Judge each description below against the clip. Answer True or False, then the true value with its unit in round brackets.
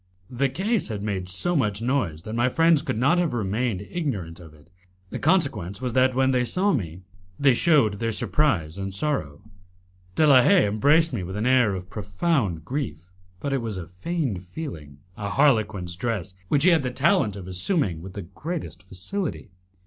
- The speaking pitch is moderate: False (115 Hz)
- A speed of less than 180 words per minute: False (185 wpm)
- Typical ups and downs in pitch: False (7.5 semitones)